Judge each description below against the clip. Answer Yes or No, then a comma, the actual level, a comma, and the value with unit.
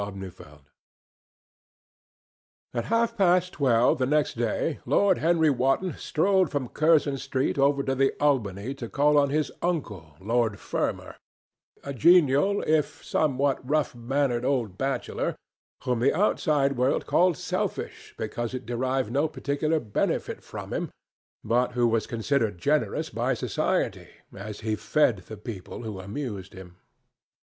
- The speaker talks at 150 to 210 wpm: No, average, 140 wpm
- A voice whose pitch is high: No, low, 135 Hz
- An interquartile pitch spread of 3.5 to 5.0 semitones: Yes, average, 4.7 semitones